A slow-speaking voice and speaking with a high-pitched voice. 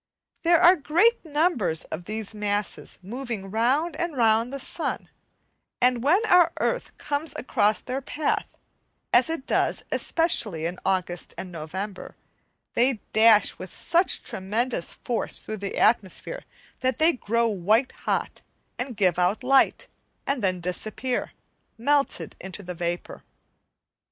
Yes: slow, 130 wpm; high, 230 Hz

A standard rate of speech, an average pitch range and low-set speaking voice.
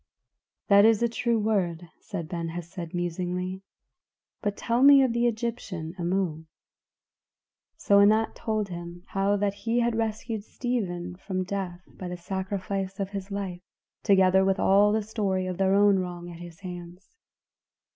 No: average, 155 wpm; average, 3.2 semitones; high, 195 Hz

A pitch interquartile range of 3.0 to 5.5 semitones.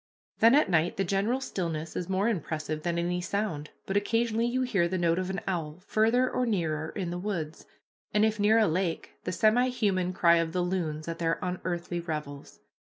Yes: average, 4.2 semitones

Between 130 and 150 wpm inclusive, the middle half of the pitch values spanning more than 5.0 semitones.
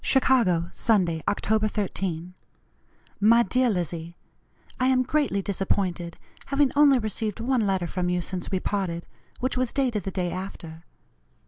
Yes: average, 140 wpm; wide, 5.4 semitones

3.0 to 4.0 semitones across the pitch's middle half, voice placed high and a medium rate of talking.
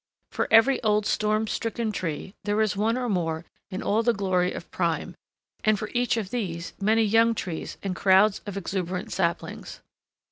Yes: average, 3.3 semitones; high, 205 Hz; average, 175 wpm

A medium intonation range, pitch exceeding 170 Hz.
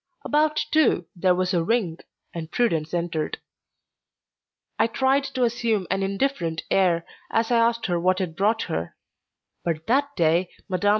No: wide, 5.8 semitones; high, 190 Hz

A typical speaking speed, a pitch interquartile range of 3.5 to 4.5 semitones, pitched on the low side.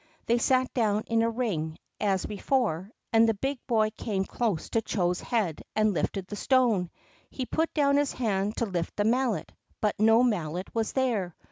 No: average, 180 wpm; average, 4.1 semitones; high, 220 Hz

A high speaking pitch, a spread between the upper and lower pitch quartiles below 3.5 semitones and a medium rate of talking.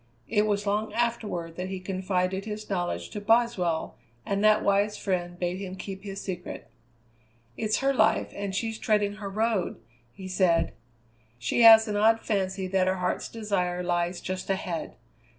Yes: high, 195 Hz; average, 2.7 semitones; average, 165 wpm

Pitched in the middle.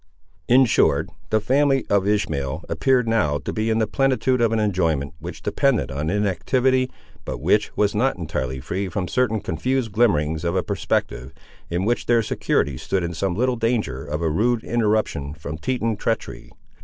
No: low, 105 Hz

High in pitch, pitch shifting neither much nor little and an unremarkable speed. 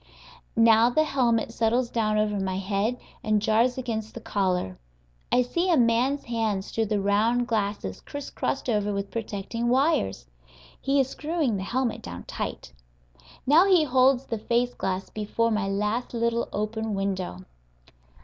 Yes: high, 225 Hz; average, 3.5 semitones; average, 150 wpm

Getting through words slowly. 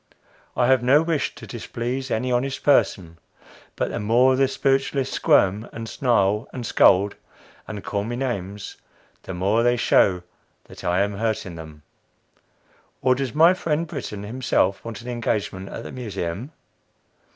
No: average, 150 wpm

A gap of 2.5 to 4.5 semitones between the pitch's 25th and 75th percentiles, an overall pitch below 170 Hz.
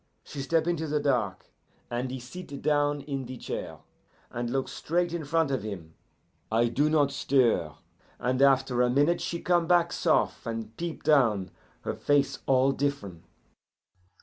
Yes: average, 4.0 semitones; low, 135 Hz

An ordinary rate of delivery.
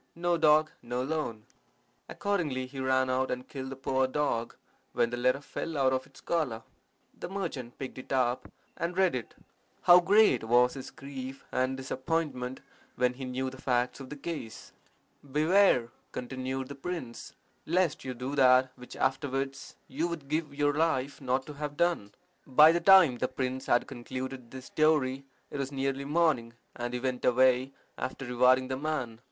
Yes: average, 170 wpm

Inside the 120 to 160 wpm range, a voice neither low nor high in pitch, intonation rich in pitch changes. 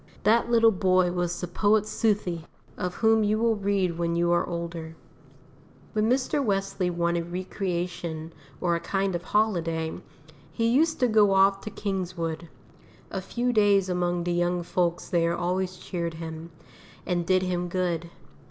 No: average, 155 wpm; medium, 180 Hz; average, 3.0 semitones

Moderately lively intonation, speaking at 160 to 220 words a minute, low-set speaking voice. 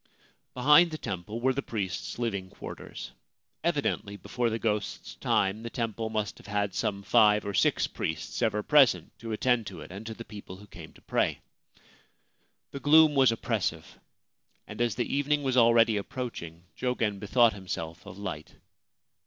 Yes: average, 3.6 semitones; average, 165 wpm; low, 110 Hz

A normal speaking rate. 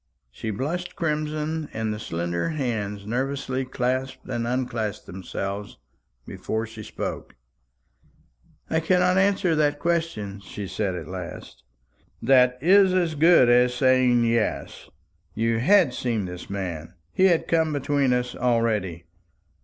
No: slow, 130 wpm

